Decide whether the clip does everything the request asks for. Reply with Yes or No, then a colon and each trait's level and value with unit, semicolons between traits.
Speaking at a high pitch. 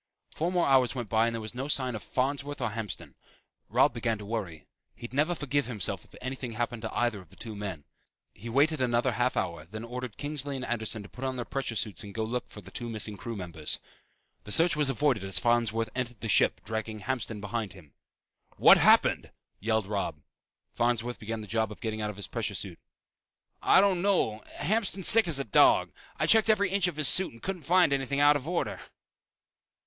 No: low, 120 Hz